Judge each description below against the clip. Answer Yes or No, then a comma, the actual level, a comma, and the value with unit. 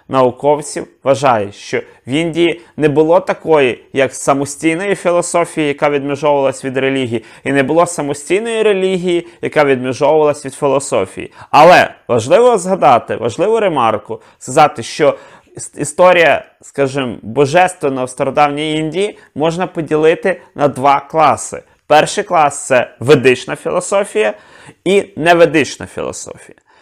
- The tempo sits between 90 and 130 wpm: Yes, average, 110 wpm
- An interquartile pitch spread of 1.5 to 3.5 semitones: No, average, 3.9 semitones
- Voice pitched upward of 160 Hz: No, medium, 150 Hz